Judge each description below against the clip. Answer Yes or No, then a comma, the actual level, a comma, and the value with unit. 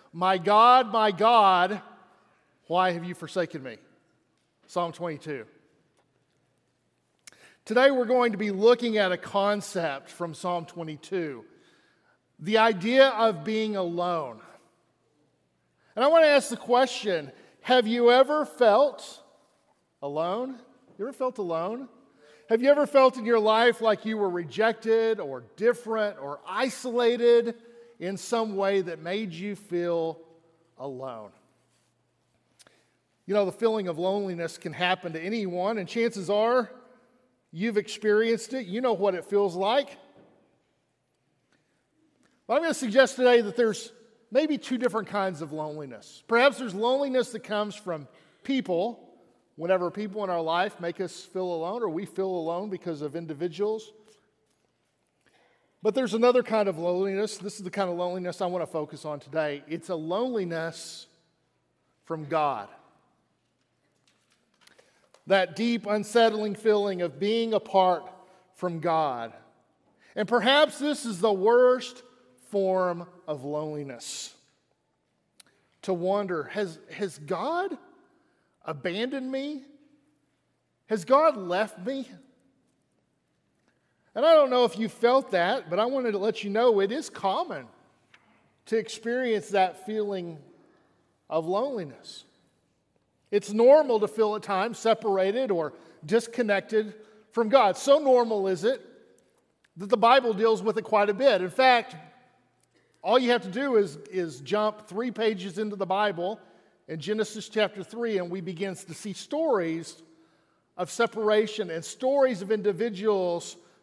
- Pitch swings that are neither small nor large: Yes, average, 5.0 semitones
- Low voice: No, high, 210 Hz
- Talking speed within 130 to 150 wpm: Yes, slow, 135 wpm